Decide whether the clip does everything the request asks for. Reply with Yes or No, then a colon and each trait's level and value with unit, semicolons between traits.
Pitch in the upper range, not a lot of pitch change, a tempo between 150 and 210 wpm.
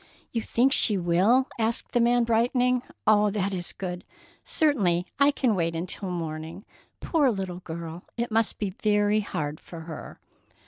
No: high, 205 Hz; average, 5.1 semitones; average, 165 wpm